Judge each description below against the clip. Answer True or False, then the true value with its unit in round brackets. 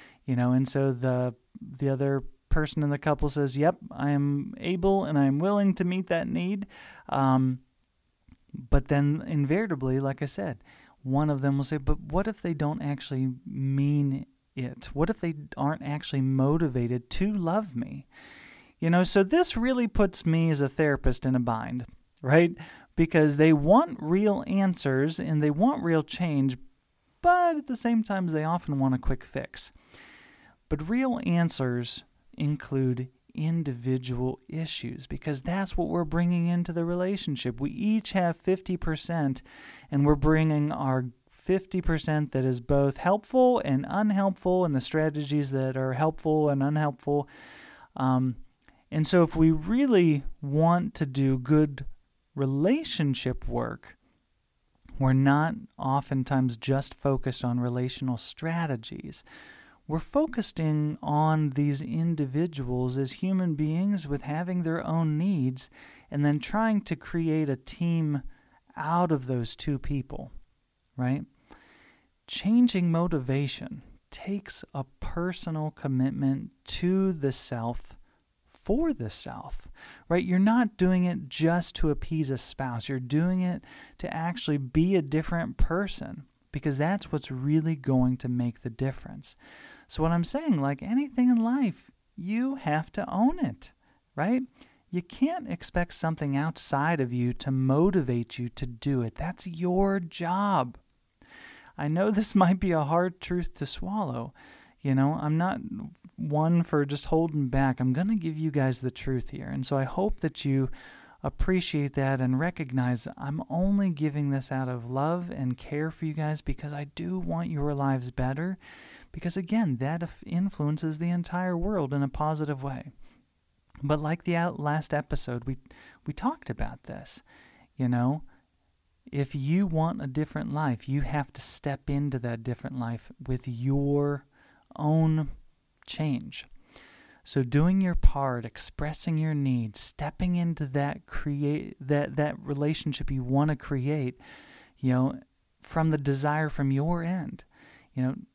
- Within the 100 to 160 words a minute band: True (150 wpm)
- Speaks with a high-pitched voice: False (150 Hz)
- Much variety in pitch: False (4.5 semitones)